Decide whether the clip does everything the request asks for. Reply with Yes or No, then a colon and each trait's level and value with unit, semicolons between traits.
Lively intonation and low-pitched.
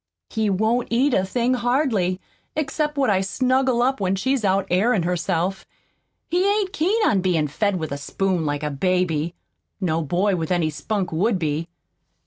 No: wide, 6.2 semitones; high, 195 Hz